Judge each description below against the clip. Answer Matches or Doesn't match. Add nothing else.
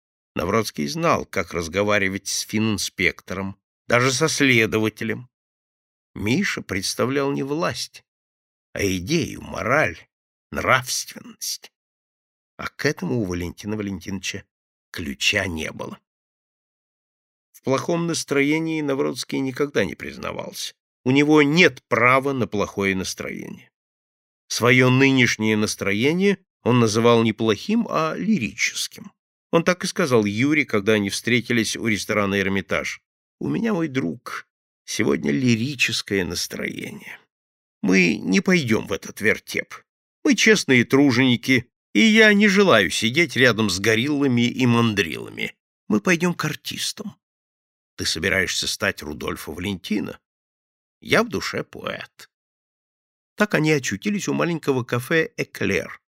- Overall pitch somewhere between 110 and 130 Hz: Matches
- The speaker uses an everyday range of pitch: Doesn't match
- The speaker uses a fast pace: Doesn't match